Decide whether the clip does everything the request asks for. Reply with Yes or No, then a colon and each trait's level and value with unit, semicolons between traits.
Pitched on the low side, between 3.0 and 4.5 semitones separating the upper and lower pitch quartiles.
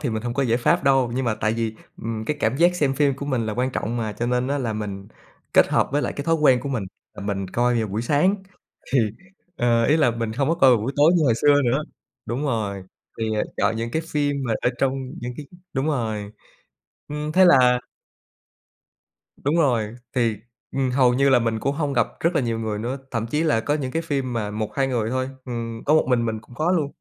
Yes: low, 125 Hz; average, 3.9 semitones